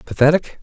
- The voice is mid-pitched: Yes, medium, 145 Hz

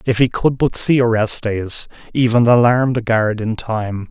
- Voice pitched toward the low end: Yes, low, 115 Hz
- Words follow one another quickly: No, average, 175 wpm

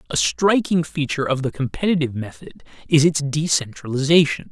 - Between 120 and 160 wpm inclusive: Yes, slow, 135 wpm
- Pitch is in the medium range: Yes, medium, 145 Hz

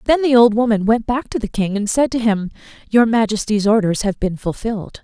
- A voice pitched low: No, high, 220 Hz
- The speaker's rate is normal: No, fast, 225 wpm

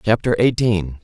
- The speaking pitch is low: Yes, low, 105 Hz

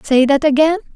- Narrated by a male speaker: No, female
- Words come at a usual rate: Yes, average, 190 wpm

